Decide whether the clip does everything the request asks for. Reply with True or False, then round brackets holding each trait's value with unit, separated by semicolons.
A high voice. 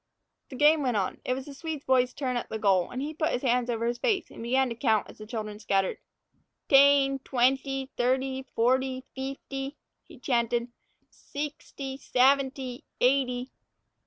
True (260 Hz)